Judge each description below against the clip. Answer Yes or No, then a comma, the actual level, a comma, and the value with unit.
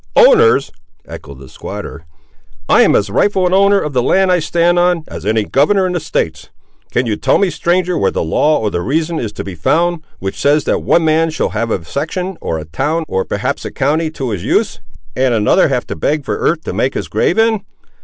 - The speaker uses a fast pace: Yes, fast, 225 wpm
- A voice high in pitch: No, medium, 155 Hz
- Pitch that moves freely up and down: Yes, wide, 8.2 semitones